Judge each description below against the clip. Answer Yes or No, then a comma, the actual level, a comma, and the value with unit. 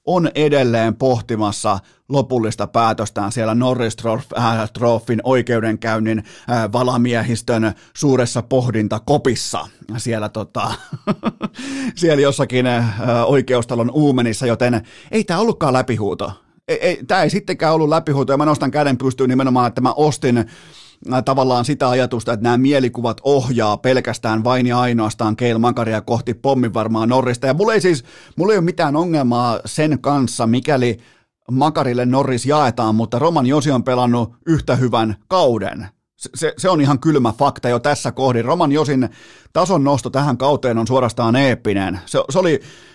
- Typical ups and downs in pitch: Yes, average, 3.3 semitones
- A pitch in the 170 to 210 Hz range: No, low, 125 Hz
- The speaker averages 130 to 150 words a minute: Yes, average, 140 wpm